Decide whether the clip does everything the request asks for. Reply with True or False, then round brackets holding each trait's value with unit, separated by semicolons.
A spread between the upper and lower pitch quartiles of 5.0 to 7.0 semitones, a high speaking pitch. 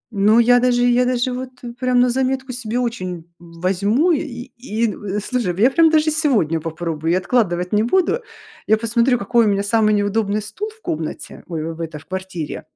True (5.3 semitones; 225 Hz)